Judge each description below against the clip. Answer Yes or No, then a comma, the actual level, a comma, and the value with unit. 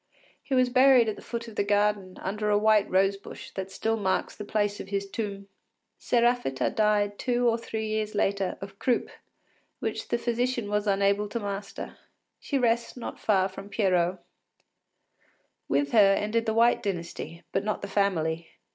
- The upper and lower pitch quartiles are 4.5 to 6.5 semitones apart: No, narrow, 2.6 semitones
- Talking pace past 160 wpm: Yes, average, 170 wpm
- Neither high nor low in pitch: No, high, 205 Hz